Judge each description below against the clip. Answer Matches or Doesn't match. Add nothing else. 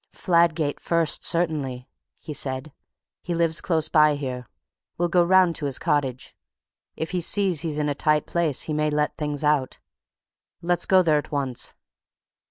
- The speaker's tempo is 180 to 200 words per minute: Doesn't match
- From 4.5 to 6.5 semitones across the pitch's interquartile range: Doesn't match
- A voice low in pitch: Doesn't match